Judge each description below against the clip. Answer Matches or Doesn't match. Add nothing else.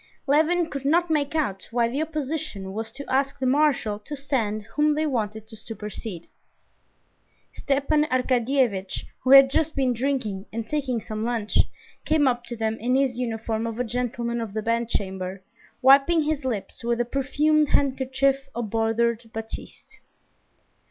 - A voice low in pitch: Doesn't match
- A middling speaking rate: Matches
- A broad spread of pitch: Doesn't match